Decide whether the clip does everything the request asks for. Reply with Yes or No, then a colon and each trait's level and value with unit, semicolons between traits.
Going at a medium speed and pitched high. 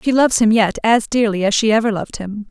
No: fast, 265 wpm; high, 220 Hz